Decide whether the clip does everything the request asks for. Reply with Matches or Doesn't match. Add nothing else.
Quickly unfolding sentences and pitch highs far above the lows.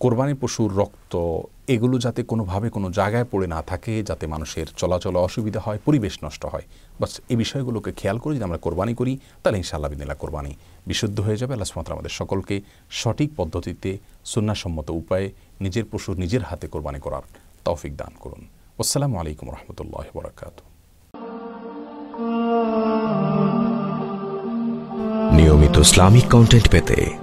Matches